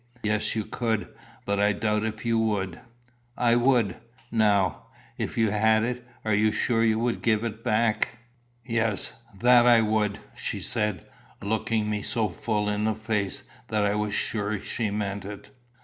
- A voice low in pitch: Yes, low, 110 Hz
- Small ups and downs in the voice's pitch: Yes, narrow, 1.5 semitones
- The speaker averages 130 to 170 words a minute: Yes, average, 165 wpm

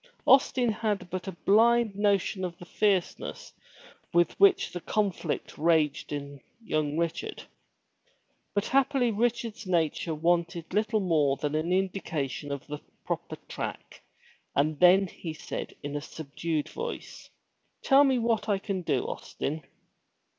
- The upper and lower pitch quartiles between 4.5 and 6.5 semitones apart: Yes, wide, 5.5 semitones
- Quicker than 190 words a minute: No, slow, 135 wpm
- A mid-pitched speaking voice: Yes, medium, 180 Hz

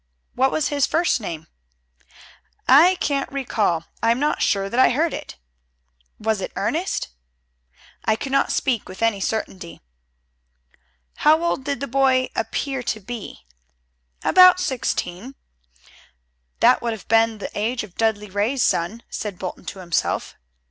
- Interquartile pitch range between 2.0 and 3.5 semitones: No, average, 5.1 semitones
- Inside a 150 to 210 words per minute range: No, average, 140 wpm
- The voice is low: No, high, 230 Hz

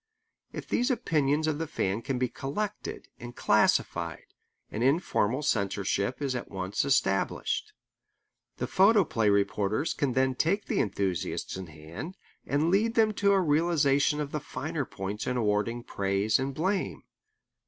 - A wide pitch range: Yes, wide, 7.5 semitones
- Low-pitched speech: Yes, low, 130 Hz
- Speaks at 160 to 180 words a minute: No, average, 145 wpm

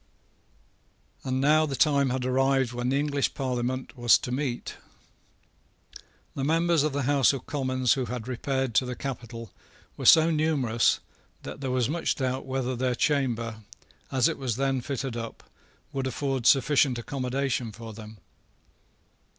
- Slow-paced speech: No, average, 150 wpm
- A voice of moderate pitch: No, low, 130 Hz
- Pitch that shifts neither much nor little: No, narrow, 2.2 semitones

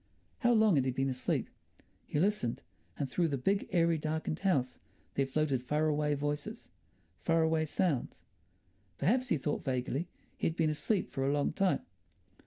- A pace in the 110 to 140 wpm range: No, average, 170 wpm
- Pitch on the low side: No, medium, 155 Hz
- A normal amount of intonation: Yes, average, 3.7 semitones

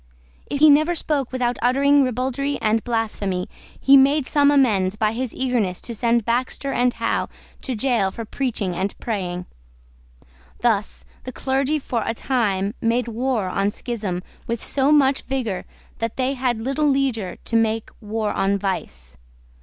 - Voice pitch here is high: Yes, high, 235 Hz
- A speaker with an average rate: Yes, average, 155 wpm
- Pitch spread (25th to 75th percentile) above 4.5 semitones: No, average, 4.2 semitones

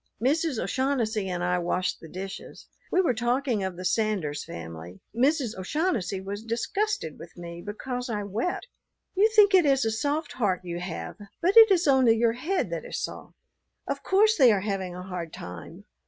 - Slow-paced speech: No, average, 185 wpm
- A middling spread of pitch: No, wide, 7.7 semitones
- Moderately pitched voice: No, high, 225 Hz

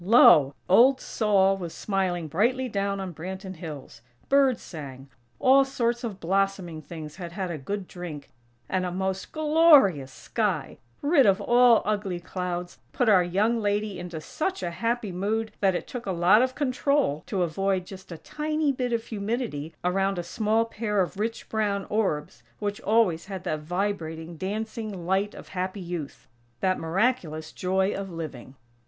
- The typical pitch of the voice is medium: No, high, 195 Hz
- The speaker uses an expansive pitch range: No, average, 4.3 semitones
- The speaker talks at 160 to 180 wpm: Yes, average, 165 wpm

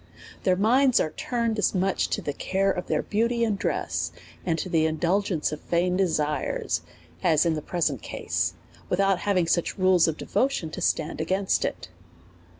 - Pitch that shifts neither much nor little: Yes, average, 3.7 semitones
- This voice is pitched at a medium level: Yes, medium, 180 Hz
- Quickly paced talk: No, average, 165 wpm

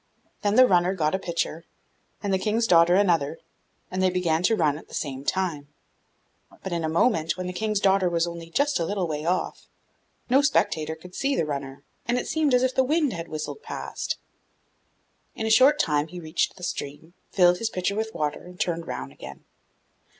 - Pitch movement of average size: Yes, average, 4.9 semitones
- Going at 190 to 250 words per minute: Yes, average, 200 wpm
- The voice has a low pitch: No, medium, 180 Hz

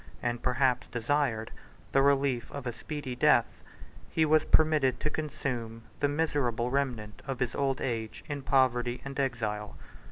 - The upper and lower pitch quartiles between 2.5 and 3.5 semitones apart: Yes, average, 3.0 semitones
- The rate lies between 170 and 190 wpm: No, average, 150 wpm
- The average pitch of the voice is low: Yes, low, 130 Hz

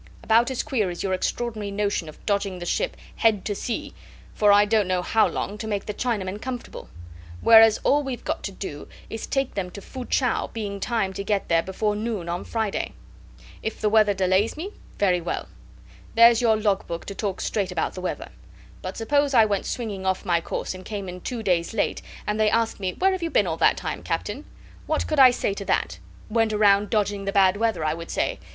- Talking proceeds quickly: Yes, fast, 225 wpm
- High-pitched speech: Yes, high, 210 Hz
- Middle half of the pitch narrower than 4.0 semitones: Yes, average, 3.0 semitones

